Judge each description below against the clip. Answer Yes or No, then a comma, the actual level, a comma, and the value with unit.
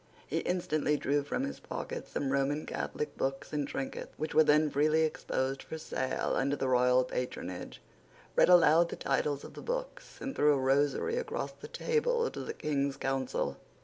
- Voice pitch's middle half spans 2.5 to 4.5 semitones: Yes, average, 4.1 semitones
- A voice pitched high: No, medium, 150 Hz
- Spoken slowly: No, average, 180 wpm